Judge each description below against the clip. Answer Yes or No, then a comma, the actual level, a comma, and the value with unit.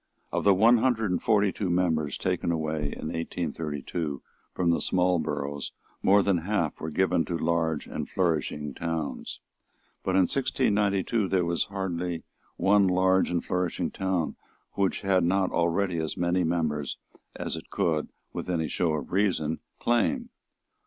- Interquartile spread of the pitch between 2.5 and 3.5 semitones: Yes, average, 3.1 semitones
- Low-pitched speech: Yes, very low, 90 Hz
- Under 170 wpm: Yes, average, 150 wpm